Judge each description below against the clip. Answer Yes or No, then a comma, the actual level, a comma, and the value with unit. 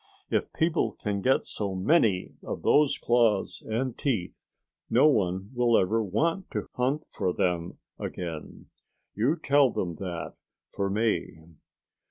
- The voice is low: Yes, low, 110 Hz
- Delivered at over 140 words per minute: No, slow, 135 wpm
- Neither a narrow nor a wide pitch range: No, wide, 6.1 semitones